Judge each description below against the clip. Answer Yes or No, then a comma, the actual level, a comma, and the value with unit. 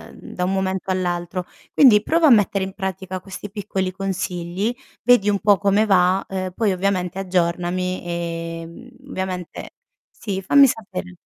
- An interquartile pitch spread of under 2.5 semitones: Yes, narrow, 2.1 semitones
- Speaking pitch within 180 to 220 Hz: Yes, high, 190 Hz